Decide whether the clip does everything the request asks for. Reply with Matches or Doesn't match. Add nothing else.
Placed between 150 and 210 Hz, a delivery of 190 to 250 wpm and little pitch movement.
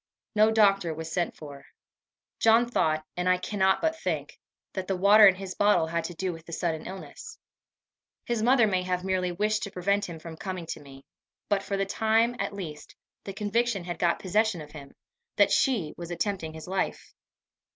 Doesn't match